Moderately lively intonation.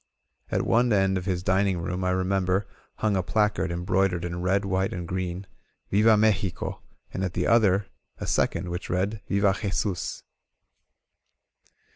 No: narrow, 1.7 semitones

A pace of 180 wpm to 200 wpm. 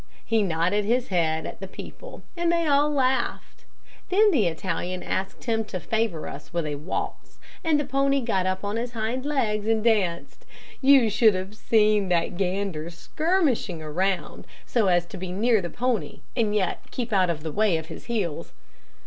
Yes: average, 185 wpm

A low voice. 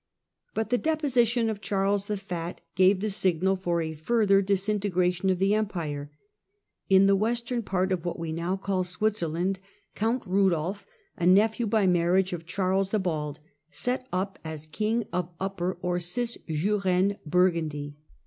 No: high, 190 Hz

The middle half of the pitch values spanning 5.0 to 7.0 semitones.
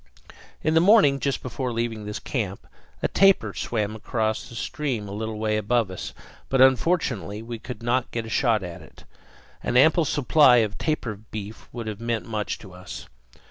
No: average, 3.6 semitones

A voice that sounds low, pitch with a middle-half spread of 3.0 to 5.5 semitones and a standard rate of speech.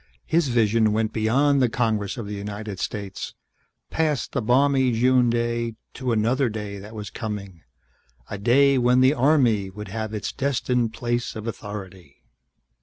Yes: low, 115 Hz; average, 3.3 semitones; average, 155 wpm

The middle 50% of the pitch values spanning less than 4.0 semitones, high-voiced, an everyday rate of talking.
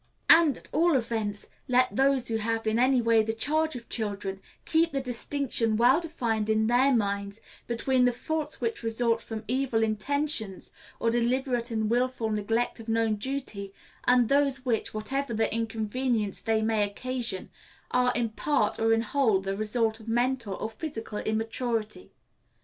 Yes: average, 2.9 semitones; high, 230 Hz; average, 160 wpm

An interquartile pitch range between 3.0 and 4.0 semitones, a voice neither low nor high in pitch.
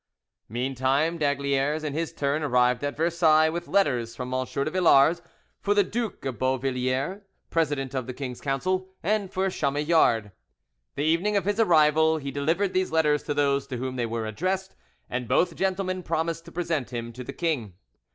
No: average, 4.8 semitones; medium, 150 Hz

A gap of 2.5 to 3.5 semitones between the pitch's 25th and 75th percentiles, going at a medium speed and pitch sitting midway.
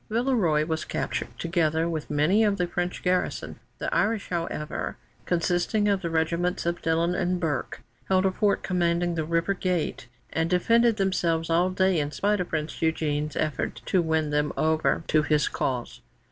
Yes: average, 2.8 semitones; average, 175 wpm; medium, 170 Hz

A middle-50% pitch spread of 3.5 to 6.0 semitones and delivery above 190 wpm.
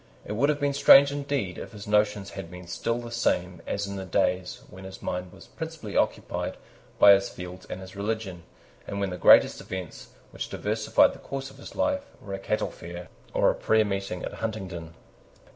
Yes: average, 4.4 semitones; average, 200 wpm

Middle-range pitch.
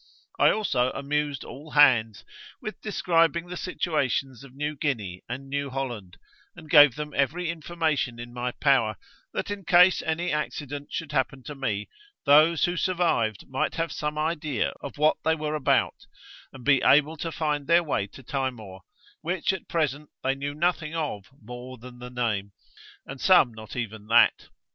Yes: medium, 145 Hz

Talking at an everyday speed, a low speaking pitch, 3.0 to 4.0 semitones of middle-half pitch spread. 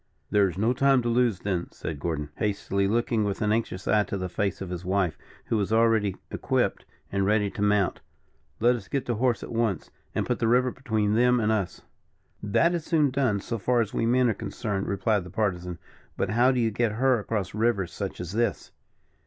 No: fast, 215 wpm; low, 110 Hz; average, 3.4 semitones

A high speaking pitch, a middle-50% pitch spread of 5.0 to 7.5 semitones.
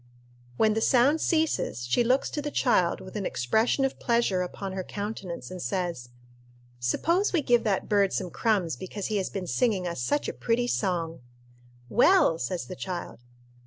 Yes: high, 200 Hz; average, 5.3 semitones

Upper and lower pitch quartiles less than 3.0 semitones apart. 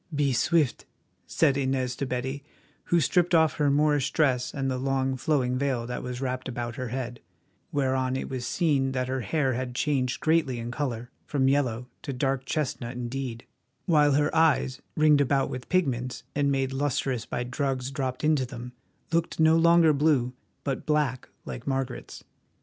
Yes: narrow, 2.6 semitones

